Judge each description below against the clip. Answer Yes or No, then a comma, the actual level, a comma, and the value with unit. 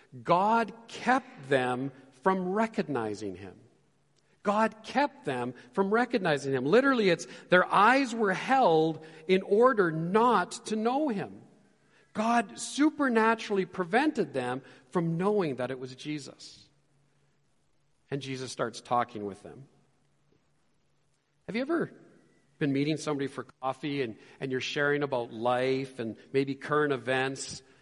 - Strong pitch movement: Yes, wide, 8.9 semitones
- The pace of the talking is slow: Yes, slow, 125 wpm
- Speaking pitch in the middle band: Yes, medium, 155 Hz